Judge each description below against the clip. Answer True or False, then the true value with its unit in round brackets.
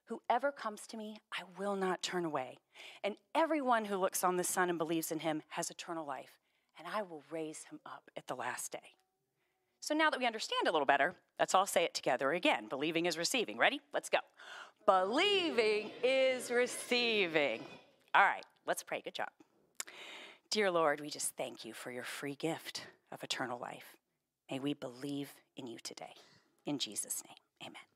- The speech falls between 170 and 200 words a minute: True (180 wpm)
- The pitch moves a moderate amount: False (8.2 semitones)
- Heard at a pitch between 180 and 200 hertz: True (190 Hz)